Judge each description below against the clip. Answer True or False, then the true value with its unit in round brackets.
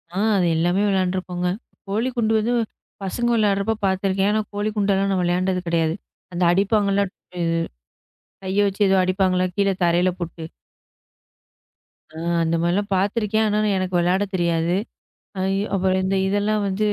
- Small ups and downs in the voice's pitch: True (2.2 semitones)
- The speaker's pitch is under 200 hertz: True (190 Hz)